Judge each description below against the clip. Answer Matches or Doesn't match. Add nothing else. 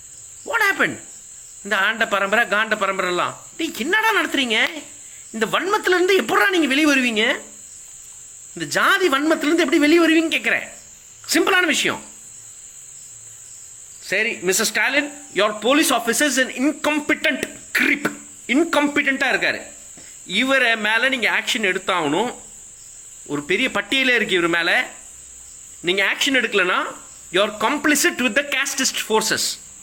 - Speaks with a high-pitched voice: Matches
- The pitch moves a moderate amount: Doesn't match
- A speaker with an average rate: Matches